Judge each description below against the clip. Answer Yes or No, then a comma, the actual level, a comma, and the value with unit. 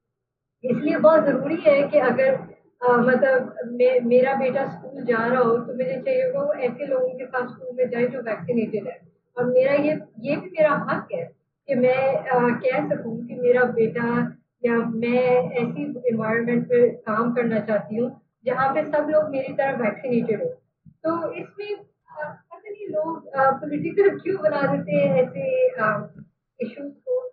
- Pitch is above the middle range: Yes, very high, 255 Hz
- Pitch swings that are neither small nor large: Yes, average, 3.1 semitones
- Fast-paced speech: No, average, 160 wpm